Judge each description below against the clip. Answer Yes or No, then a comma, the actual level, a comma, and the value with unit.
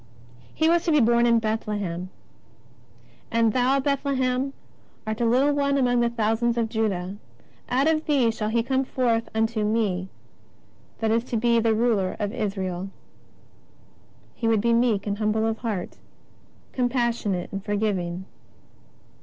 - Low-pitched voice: No, high, 225 Hz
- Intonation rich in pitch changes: No, average, 2.9 semitones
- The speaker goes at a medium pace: Yes, average, 160 wpm